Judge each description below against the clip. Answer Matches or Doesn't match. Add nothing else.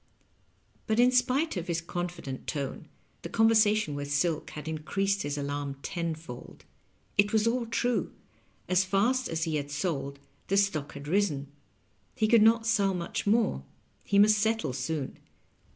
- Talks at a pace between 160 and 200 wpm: Doesn't match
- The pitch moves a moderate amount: Doesn't match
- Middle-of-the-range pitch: Matches